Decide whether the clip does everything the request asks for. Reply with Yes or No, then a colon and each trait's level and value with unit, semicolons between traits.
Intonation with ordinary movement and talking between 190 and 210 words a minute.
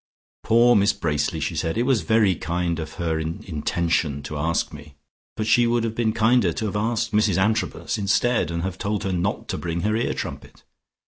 Yes: average, 4.9 semitones; fast, 205 wpm